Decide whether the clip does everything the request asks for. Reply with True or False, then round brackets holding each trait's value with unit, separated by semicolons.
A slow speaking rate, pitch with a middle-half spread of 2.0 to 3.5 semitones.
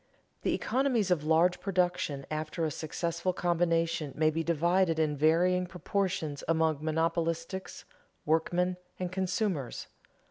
True (115 wpm; 2.4 semitones)